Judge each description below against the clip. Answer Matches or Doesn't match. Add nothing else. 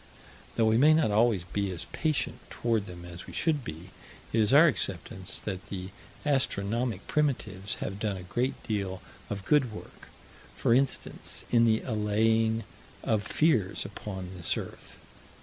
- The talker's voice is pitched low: Matches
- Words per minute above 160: Doesn't match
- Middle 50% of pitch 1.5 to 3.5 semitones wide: Doesn't match